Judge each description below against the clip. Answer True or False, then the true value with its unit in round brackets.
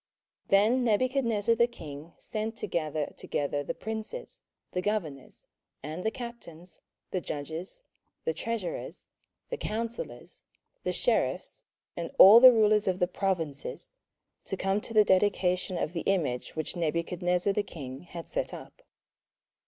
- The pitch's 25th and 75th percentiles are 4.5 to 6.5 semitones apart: True (5.0 semitones)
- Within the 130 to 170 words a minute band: True (140 wpm)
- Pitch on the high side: True (195 Hz)